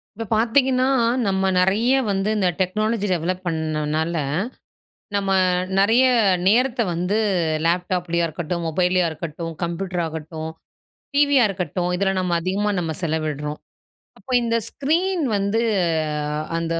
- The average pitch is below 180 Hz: No, medium, 185 Hz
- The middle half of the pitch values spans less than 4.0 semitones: No, average, 4.3 semitones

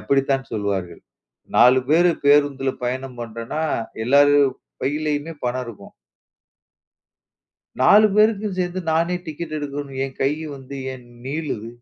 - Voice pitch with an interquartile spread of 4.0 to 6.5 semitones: No, average, 3.6 semitones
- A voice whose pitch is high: No, medium, 140 Hz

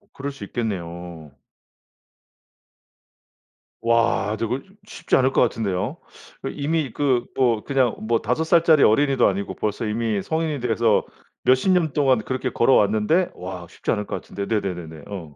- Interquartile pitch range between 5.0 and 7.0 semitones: Yes, average, 5.3 semitones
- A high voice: No, low, 115 Hz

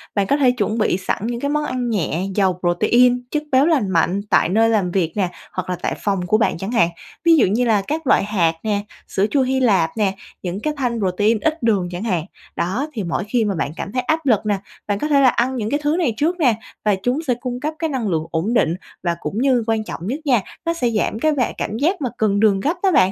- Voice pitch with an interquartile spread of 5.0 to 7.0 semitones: Yes, average, 5.3 semitones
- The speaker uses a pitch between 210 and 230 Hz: Yes, high, 225 Hz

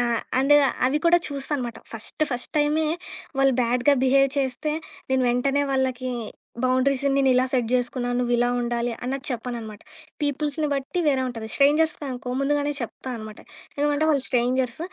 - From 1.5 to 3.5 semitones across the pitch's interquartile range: Yes, average, 2.7 semitones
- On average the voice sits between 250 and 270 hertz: Yes, very high, 260 Hz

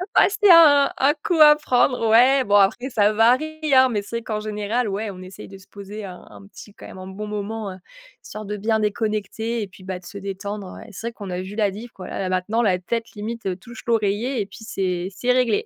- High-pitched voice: Yes, high, 210 Hz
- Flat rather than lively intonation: No, average, 3.3 semitones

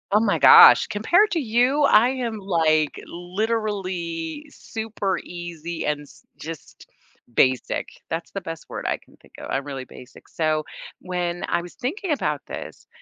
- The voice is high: No, medium, 180 Hz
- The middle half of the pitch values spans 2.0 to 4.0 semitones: No, wide, 5.6 semitones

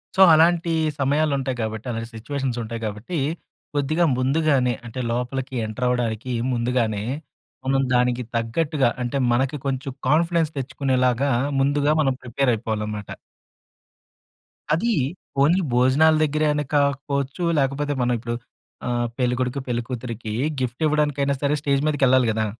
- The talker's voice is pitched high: No, low, 130 Hz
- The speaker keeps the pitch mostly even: No, average, 3.2 semitones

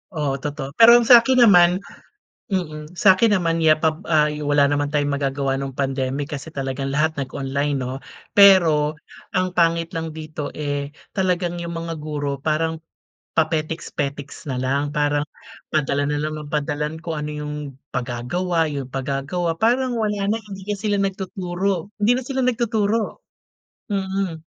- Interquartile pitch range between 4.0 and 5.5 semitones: Yes, average, 4.5 semitones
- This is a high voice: No, medium, 155 Hz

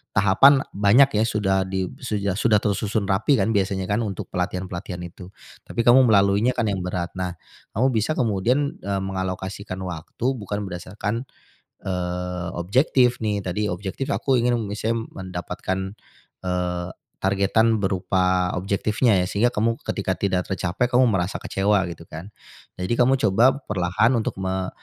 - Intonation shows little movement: No, average, 3.4 semitones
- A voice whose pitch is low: Yes, low, 100 Hz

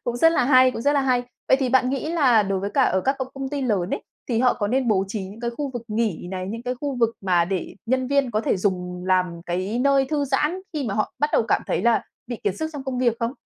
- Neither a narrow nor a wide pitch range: Yes, average, 5.0 semitones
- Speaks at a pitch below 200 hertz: No, high, 240 Hz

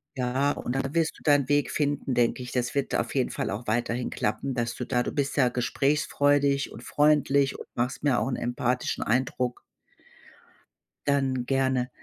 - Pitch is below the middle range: Yes, low, 130 Hz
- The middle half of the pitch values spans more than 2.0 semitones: Yes, narrow, 2.5 semitones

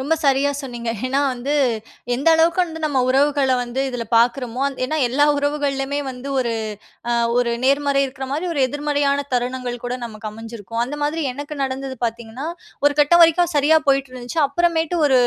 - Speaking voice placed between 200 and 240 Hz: No, very high, 275 Hz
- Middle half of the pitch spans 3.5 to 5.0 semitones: No, average, 2.7 semitones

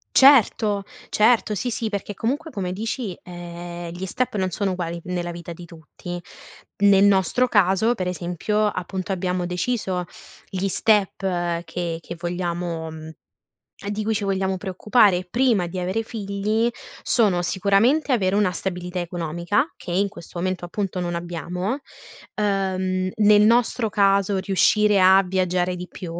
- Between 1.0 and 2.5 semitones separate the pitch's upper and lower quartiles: No, average, 2.9 semitones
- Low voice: No, high, 190 Hz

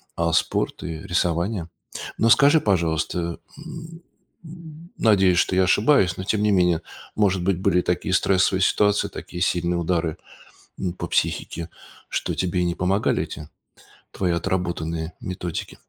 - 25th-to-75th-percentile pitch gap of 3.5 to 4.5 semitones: No, average, 3.1 semitones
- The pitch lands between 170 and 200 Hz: No, very low, 90 Hz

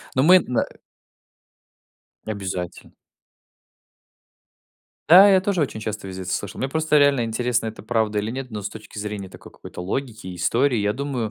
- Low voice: Yes, low, 115 Hz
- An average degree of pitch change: Yes, average, 4.9 semitones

